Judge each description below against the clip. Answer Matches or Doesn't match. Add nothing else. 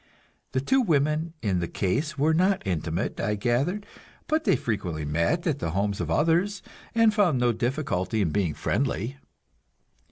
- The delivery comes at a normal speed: Matches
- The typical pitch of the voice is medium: Doesn't match